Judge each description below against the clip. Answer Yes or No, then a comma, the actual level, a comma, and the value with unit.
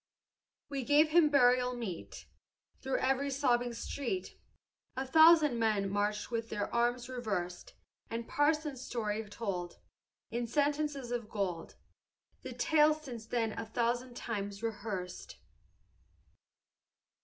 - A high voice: Yes, high, 240 Hz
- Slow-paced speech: Yes, slow, 115 wpm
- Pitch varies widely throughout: No, average, 4.4 semitones